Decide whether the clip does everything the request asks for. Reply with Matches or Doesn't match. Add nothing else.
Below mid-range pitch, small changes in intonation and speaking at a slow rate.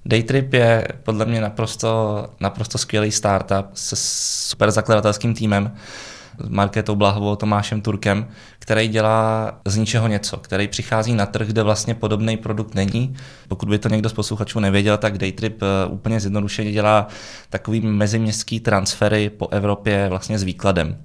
Doesn't match